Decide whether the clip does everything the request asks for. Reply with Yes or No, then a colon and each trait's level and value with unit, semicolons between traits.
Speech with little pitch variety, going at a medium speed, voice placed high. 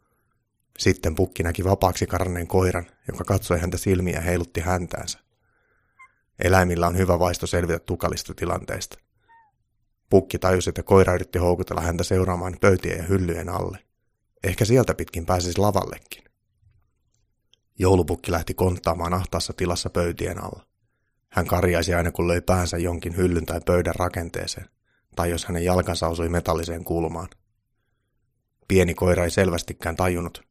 No: narrow, 2.3 semitones; average, 130 wpm; very low, 90 Hz